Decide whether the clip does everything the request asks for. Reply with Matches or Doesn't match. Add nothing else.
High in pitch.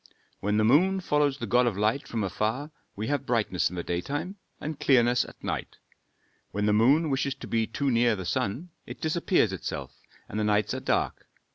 Doesn't match